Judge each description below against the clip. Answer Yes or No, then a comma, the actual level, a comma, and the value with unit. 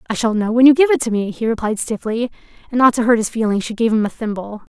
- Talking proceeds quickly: Yes, fast, 290 wpm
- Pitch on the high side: Yes, high, 230 Hz